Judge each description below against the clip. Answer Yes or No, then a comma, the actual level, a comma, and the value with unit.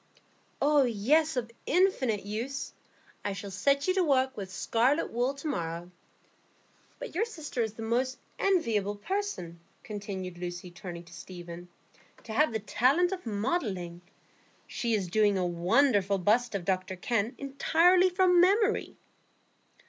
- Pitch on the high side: Yes, high, 230 Hz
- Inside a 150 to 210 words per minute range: No, average, 140 wpm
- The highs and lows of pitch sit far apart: Yes, wide, 7.4 semitones